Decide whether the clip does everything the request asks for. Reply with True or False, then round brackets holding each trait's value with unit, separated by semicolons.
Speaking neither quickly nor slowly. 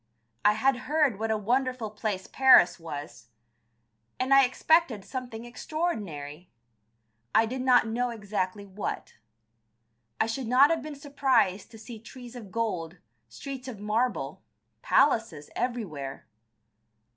False (125 wpm)